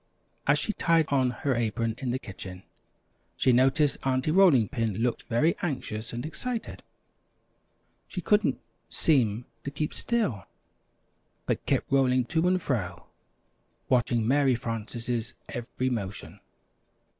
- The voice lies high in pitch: No, low, 125 Hz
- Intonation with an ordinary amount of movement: Yes, average, 4.8 semitones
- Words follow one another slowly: Yes, slow, 125 wpm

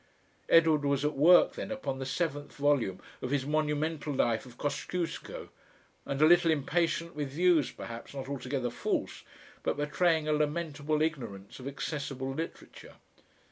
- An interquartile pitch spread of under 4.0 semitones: Yes, average, 3.1 semitones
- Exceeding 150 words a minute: No, average, 145 wpm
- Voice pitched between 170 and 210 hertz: No, medium, 145 Hz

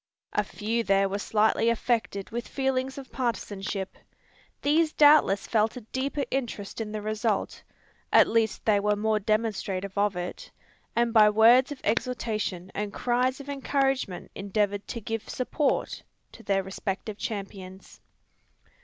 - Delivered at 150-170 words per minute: No, average, 140 wpm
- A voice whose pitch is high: Yes, high, 220 Hz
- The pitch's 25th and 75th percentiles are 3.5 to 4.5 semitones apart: Yes, average, 3.8 semitones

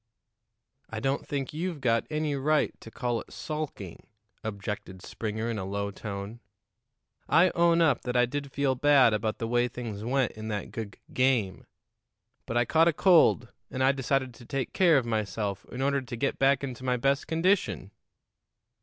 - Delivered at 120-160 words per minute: No, average, 180 wpm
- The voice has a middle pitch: No, low, 125 Hz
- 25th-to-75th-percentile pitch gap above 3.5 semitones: Yes, average, 4.2 semitones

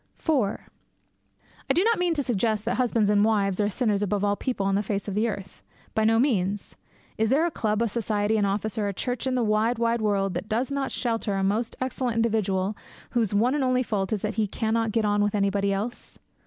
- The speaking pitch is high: Yes, high, 215 Hz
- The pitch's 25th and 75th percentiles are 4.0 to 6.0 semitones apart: No, average, 2.8 semitones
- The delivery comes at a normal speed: No, fast, 230 wpm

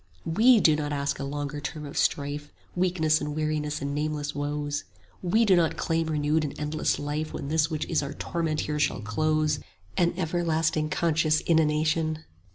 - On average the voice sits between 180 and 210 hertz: No, medium, 155 Hz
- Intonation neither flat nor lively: No, narrow, 1.6 semitones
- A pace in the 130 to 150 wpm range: No, average, 175 wpm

